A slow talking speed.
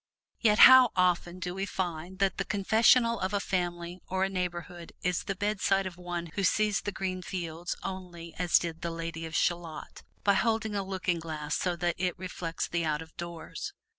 No: average, 195 wpm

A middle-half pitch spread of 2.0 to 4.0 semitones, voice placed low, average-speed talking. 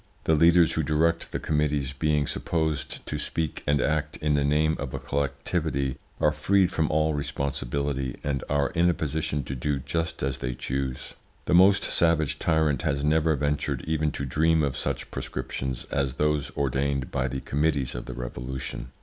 Yes: narrow, 2.5 semitones; very low, 75 Hz; average, 175 wpm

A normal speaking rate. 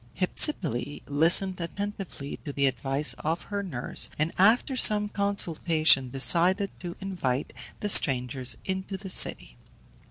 No: slow, 125 wpm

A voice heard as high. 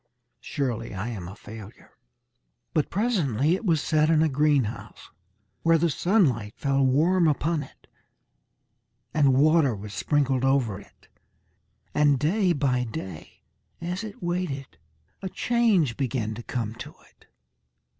No: medium, 140 Hz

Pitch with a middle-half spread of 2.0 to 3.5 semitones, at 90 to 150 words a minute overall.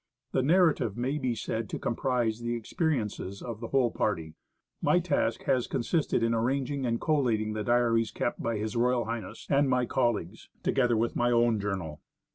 No: average, 2.7 semitones; average, 165 wpm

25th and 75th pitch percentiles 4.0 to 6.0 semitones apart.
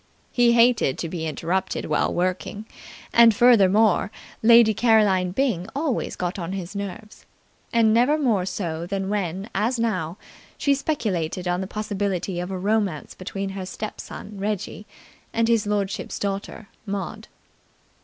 No: average, 3.4 semitones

